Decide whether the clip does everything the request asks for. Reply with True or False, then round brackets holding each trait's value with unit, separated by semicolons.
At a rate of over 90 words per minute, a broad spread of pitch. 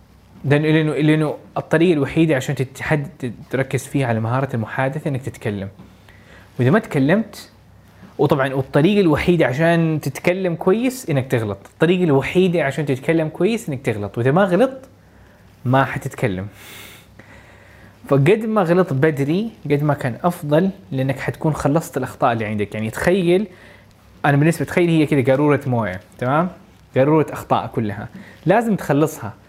True (130 wpm; 6.5 semitones)